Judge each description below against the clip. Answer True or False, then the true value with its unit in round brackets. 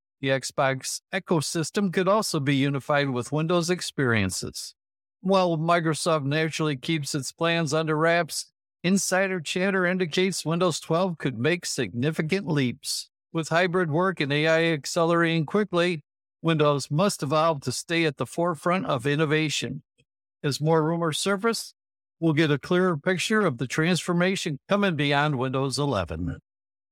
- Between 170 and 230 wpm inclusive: False (135 wpm)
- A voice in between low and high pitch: True (160 Hz)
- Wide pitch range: False (3.9 semitones)